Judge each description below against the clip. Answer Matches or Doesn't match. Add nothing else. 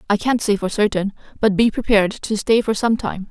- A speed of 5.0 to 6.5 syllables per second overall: Matches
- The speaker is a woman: Matches